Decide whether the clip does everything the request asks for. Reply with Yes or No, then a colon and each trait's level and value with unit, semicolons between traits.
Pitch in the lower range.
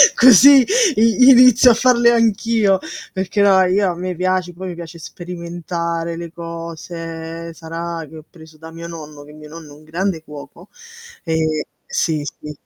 No: medium, 170 Hz